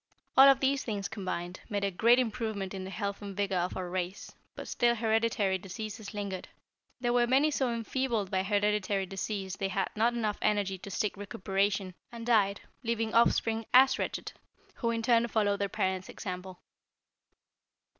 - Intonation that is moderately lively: Yes, average, 3.2 semitones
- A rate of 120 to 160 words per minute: No, average, 170 wpm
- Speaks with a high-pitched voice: Yes, high, 205 Hz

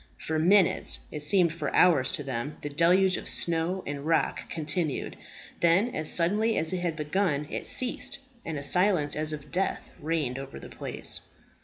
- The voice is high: No, medium, 165 Hz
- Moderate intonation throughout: Yes, average, 3.6 semitones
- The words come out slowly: No, average, 175 wpm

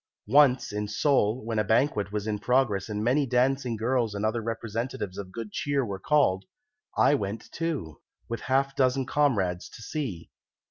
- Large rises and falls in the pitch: No, average, 4.4 semitones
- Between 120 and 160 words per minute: No, average, 175 wpm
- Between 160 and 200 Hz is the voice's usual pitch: No, low, 115 Hz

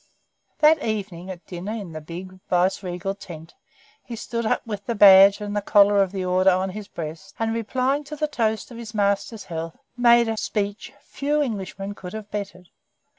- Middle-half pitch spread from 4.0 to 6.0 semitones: No, average, 3.3 semitones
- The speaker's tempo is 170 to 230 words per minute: Yes, average, 185 wpm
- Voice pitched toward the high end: Yes, high, 205 Hz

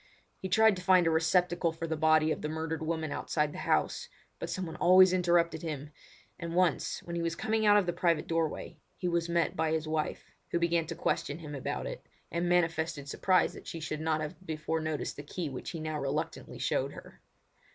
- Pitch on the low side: No, medium, 165 Hz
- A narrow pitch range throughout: Yes, narrow, 1.9 semitones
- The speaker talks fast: Yes, fast, 215 wpm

